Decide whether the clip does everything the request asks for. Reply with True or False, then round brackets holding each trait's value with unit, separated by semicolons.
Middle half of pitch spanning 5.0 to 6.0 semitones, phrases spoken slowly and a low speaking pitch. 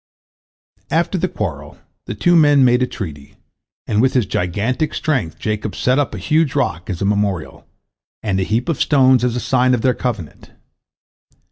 False (5.3 semitones; 175 wpm; 125 Hz)